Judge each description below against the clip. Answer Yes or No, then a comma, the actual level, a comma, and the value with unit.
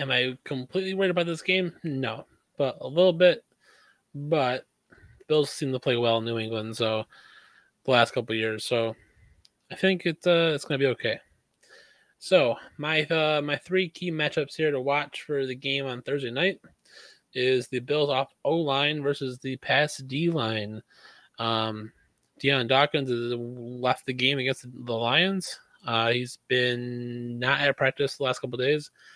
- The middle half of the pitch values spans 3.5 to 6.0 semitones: Yes, average, 4.0 semitones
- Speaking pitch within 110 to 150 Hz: Yes, low, 135 Hz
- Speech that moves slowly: No, average, 175 wpm